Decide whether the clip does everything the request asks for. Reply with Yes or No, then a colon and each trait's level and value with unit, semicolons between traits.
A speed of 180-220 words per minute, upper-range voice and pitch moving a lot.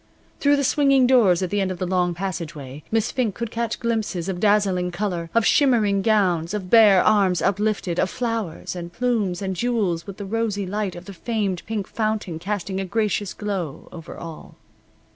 No: average, 185 wpm; high, 200 Hz; average, 3.7 semitones